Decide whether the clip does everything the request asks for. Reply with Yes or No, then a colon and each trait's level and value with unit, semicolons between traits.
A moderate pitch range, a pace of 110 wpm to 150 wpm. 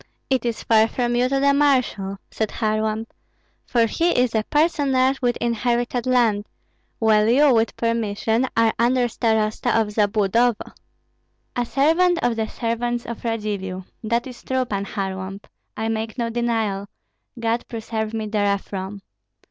No: narrow, 2.3 semitones; average, 145 wpm